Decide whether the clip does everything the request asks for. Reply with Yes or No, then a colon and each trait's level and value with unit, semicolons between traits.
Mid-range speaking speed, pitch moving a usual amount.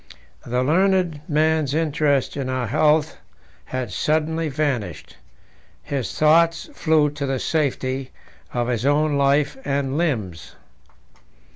No: slow, 115 wpm; average, 3.3 semitones